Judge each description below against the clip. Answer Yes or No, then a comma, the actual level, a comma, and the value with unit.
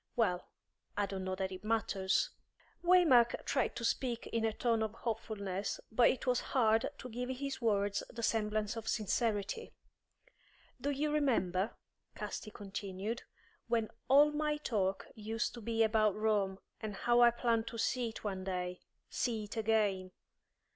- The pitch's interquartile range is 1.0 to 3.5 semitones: Yes, average, 3.1 semitones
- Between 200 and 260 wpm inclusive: No, average, 155 wpm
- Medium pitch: No, high, 220 Hz